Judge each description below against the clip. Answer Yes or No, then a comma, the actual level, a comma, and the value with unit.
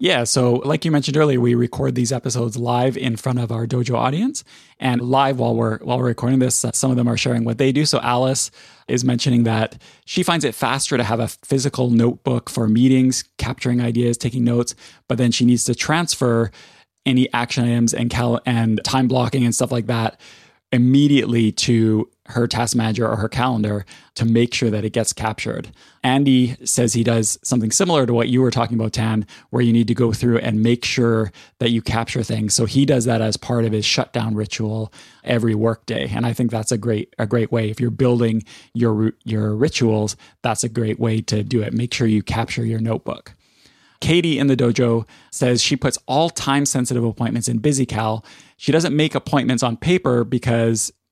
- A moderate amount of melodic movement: No, narrow, 2.0 semitones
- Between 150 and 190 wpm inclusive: No, fast, 205 wpm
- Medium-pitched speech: No, low, 120 Hz